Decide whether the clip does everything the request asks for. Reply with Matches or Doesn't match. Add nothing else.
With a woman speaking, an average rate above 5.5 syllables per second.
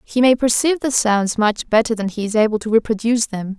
Matches